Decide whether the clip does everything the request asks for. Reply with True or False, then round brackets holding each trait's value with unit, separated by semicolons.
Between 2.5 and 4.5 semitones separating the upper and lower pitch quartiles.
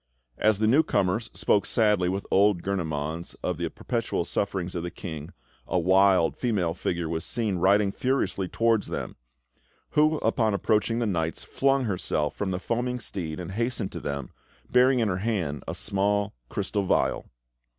True (4.2 semitones)